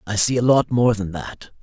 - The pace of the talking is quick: Yes, fast, 260 wpm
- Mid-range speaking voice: No, low, 110 Hz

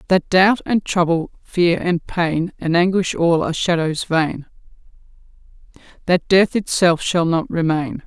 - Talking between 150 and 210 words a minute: No, average, 140 wpm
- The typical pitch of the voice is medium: Yes, medium, 170 Hz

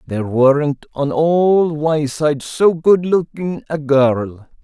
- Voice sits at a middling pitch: Yes, medium, 150 Hz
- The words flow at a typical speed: No, slow, 130 wpm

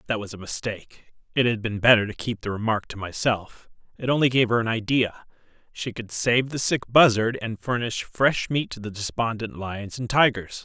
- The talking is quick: No, average, 190 wpm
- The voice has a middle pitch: No, low, 115 Hz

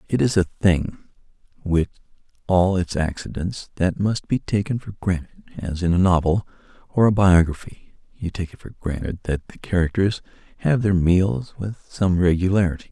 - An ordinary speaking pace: Yes, average, 165 wpm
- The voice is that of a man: Yes, male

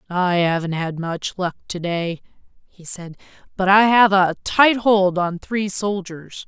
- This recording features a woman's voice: Yes, female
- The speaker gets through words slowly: No, average, 165 wpm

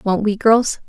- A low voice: No, high, 210 Hz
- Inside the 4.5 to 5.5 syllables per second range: No, 4.1 syllables/s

